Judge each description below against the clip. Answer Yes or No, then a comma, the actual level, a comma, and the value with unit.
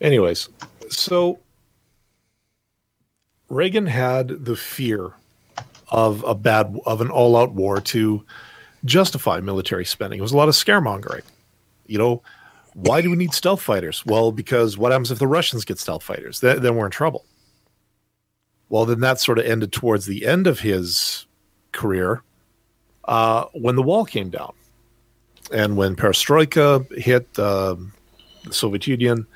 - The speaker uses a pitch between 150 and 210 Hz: No, low, 115 Hz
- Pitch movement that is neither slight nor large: Yes, average, 3.3 semitones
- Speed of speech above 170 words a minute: No, average, 150 wpm